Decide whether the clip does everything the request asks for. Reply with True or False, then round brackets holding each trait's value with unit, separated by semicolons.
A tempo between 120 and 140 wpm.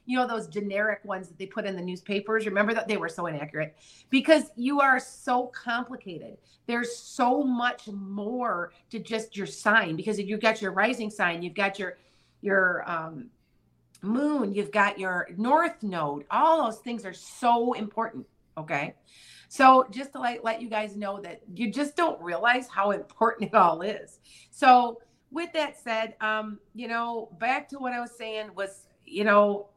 False (180 wpm)